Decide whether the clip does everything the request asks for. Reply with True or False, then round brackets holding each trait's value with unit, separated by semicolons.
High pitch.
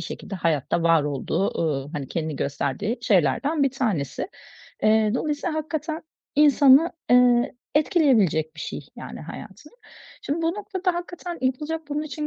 True (255 Hz)